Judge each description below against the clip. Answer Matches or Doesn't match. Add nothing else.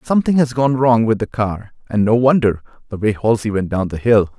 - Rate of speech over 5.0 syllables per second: Matches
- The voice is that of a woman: Doesn't match